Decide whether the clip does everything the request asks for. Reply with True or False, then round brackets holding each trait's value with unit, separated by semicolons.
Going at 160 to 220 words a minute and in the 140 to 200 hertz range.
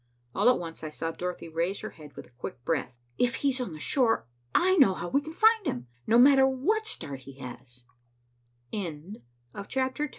True (185 wpm; 185 Hz)